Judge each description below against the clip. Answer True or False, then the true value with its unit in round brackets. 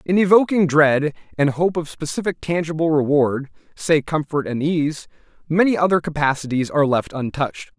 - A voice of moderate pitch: True (155 Hz)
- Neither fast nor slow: False (130 wpm)